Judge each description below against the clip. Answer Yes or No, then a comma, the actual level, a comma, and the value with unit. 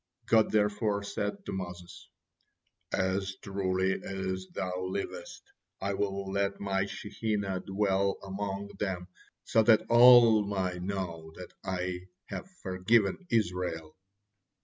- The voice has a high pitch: No, very low, 95 Hz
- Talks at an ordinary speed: No, slow, 115 wpm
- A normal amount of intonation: No, narrow, 1.8 semitones